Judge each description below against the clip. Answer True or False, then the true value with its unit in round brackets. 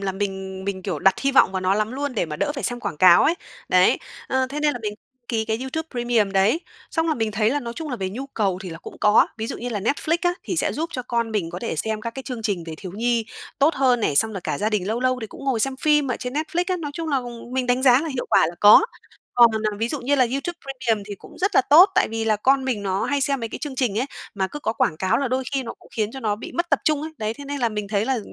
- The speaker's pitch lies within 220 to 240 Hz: True (235 Hz)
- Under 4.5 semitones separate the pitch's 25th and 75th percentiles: False (4.8 semitones)